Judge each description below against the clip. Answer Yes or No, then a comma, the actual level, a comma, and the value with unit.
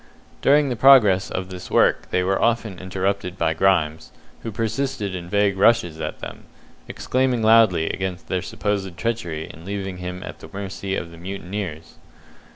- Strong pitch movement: No, average, 3.4 semitones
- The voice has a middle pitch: No, very low, 95 Hz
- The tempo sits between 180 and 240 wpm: No, average, 160 wpm